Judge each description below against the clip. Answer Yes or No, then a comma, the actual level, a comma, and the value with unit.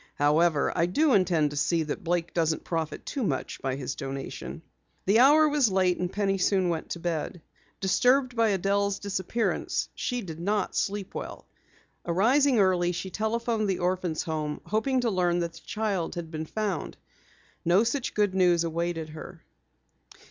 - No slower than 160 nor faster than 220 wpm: Yes, average, 165 wpm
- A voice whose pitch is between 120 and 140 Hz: No, medium, 185 Hz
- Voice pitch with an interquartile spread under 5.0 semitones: Yes, average, 4.4 semitones